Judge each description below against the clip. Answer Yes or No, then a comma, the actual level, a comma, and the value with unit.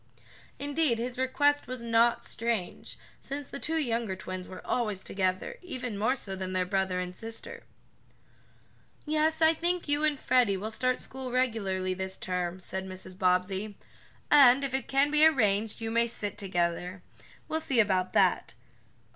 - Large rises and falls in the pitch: Yes, wide, 6.4 semitones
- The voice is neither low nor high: No, high, 230 Hz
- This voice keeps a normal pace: Yes, average, 160 wpm